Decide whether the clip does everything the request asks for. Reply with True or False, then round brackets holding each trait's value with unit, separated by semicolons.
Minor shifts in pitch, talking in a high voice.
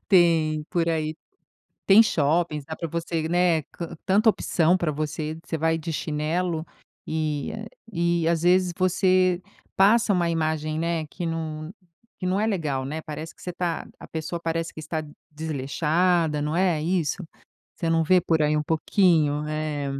False (2.3 semitones; 165 Hz)